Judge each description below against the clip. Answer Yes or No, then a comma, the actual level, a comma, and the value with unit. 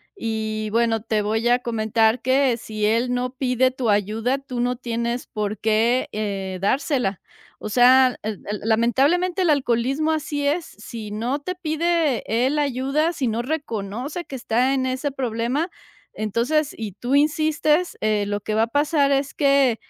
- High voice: Yes, high, 245 Hz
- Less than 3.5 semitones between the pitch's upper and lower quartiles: No, average, 4.3 semitones